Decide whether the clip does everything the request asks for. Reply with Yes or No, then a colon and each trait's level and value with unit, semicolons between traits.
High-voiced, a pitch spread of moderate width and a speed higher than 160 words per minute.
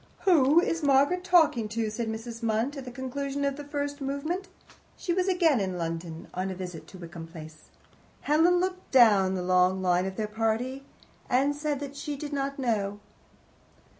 No: very high, 255 Hz; wide, 7.1 semitones; average, 180 wpm